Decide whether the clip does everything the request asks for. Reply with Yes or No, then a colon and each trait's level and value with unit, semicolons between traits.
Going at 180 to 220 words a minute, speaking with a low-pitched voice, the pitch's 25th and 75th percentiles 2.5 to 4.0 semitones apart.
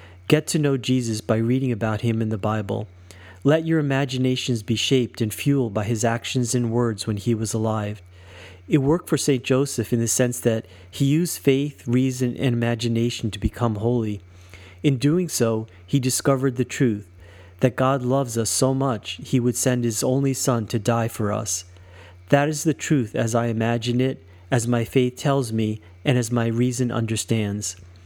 Yes: average, 185 wpm; low, 120 Hz; average, 3.3 semitones